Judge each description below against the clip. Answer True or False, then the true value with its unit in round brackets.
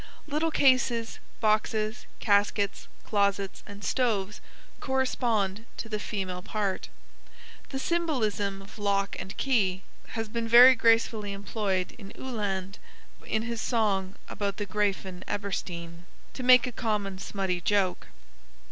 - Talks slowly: True (120 wpm)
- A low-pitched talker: False (210 Hz)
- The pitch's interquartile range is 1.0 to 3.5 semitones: True (2.9 semitones)